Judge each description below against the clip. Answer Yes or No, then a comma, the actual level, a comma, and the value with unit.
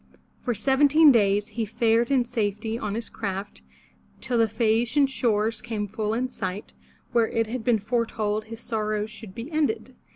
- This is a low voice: No, high, 225 Hz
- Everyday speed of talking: Yes, average, 175 wpm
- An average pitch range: No, narrow, 2.2 semitones